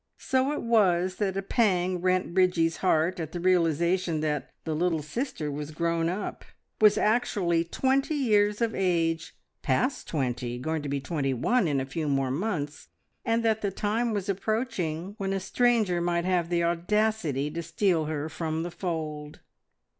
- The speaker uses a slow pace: No, average, 170 wpm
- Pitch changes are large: No, average, 4.6 semitones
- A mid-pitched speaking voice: Yes, medium, 175 Hz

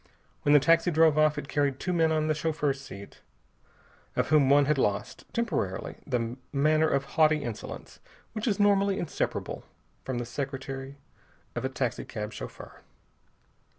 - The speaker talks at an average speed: Yes, average, 150 wpm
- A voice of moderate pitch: Yes, medium, 145 Hz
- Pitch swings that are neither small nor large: Yes, average, 3.1 semitones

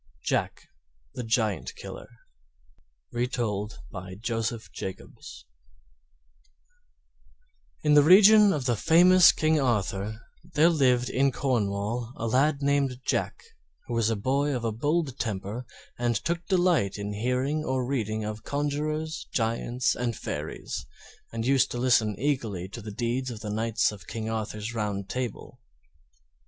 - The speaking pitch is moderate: No, low, 120 Hz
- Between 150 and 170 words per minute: No, slow, 135 wpm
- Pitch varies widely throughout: No, average, 4.6 semitones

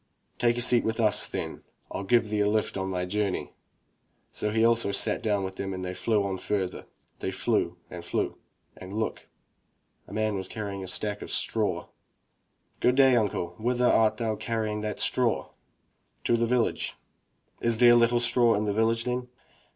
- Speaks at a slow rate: No, average, 185 wpm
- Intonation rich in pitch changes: No, average, 2.8 semitones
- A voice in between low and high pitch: No, low, 110 Hz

